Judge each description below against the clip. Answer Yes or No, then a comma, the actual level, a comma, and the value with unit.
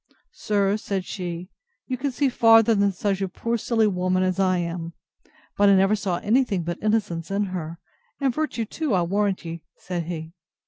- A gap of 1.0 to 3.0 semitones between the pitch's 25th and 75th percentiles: No, average, 4.0 semitones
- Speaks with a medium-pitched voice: No, high, 195 Hz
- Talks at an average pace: Yes, average, 185 wpm